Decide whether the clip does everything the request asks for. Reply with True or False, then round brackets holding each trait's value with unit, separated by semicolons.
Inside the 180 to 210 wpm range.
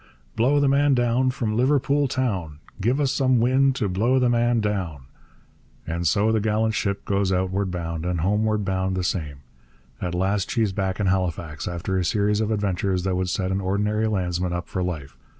True (190 wpm)